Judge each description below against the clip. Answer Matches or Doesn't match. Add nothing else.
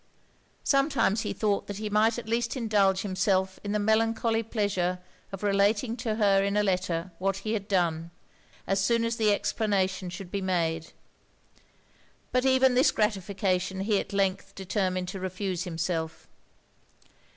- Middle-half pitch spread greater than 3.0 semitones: Doesn't match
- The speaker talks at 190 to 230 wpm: Doesn't match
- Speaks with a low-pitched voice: Doesn't match